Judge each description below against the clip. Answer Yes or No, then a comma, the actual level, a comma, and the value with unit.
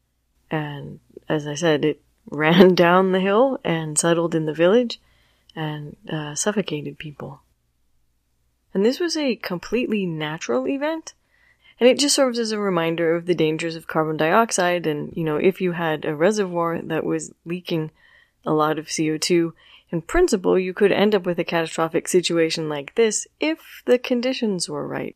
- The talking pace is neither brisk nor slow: Yes, average, 165 wpm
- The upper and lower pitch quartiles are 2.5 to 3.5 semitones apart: No, average, 4.7 semitones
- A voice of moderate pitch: Yes, medium, 170 Hz